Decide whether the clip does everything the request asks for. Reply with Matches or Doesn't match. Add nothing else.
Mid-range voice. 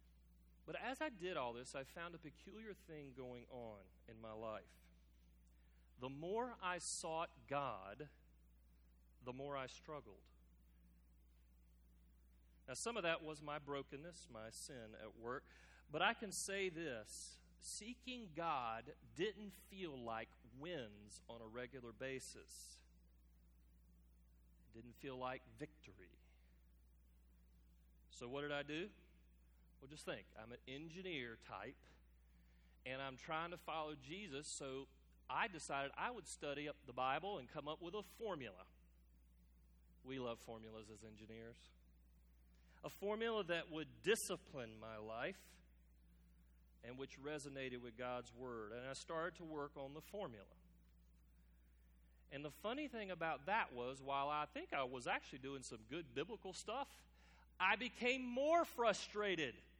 Doesn't match